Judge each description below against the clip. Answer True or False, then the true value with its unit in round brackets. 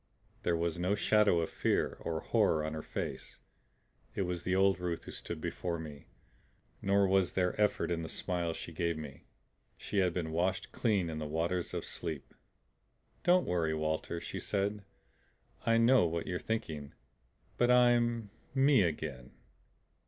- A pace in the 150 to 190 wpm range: True (160 wpm)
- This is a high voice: False (90 Hz)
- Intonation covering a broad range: False (4.0 semitones)